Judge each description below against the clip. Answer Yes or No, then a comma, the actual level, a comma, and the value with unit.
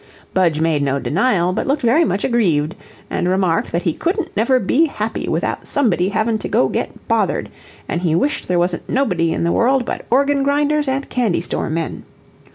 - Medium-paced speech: Yes, average, 190 wpm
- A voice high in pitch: Yes, high, 205 Hz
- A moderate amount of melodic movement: No, wide, 7.9 semitones